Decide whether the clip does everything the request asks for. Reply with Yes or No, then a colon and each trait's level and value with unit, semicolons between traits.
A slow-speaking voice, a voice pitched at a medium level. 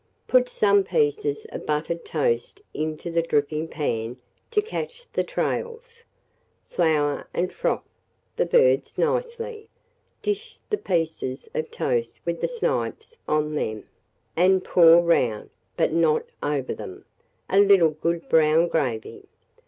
Yes: slow, 130 wpm; medium, 170 Hz